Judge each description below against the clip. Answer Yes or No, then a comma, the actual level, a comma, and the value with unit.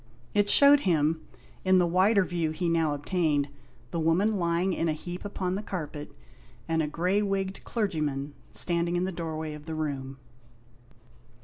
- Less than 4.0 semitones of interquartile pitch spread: Yes, average, 3.3 semitones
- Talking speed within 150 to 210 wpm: Yes, average, 165 wpm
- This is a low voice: No, medium, 170 Hz